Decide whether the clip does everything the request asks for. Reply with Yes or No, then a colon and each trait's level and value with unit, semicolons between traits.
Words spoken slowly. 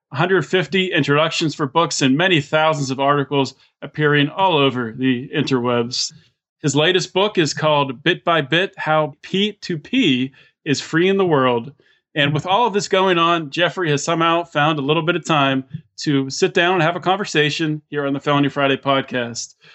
No: average, 175 wpm